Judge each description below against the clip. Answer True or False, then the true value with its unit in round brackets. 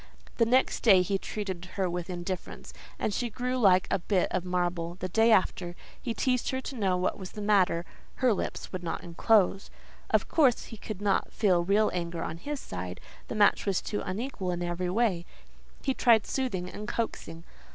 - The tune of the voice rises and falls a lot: False (4.1 semitones)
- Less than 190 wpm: False (195 wpm)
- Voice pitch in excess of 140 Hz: True (190 Hz)